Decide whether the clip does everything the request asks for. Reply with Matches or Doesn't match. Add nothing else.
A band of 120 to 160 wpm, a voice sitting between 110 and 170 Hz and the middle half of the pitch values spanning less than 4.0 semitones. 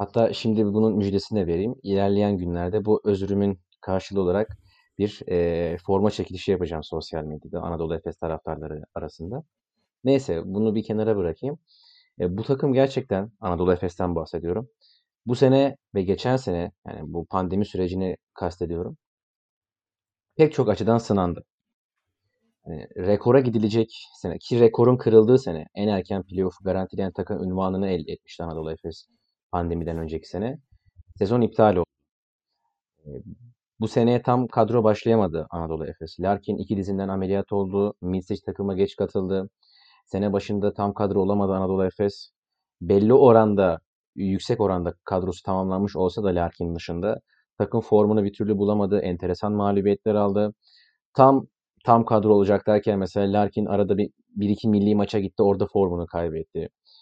Doesn't match